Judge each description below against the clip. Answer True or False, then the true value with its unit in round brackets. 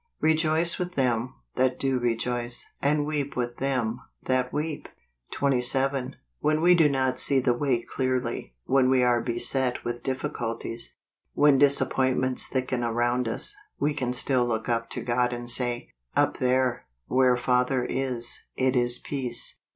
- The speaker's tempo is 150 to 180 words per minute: True (160 wpm)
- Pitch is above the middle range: False (130 Hz)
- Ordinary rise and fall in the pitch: False (1.9 semitones)